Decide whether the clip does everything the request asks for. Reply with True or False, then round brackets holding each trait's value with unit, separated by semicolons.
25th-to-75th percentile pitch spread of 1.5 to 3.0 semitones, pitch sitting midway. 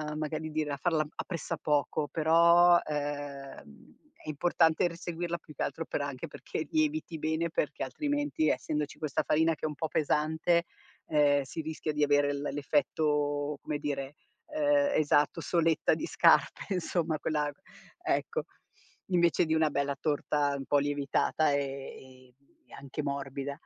True (2.5 semitones; 150 Hz)